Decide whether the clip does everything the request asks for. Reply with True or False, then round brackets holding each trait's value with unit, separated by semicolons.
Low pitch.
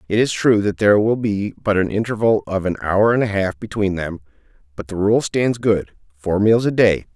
True (100 Hz)